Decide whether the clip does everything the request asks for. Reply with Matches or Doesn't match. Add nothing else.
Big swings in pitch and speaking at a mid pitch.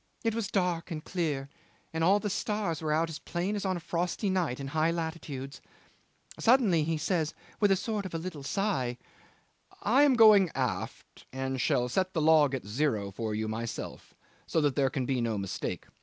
Matches